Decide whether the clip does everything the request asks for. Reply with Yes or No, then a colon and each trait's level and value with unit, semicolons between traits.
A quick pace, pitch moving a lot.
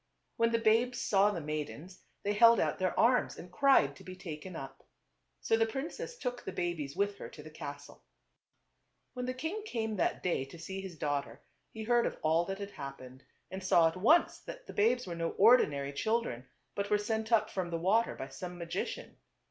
Yes: fast, 210 wpm; wide, 6.0 semitones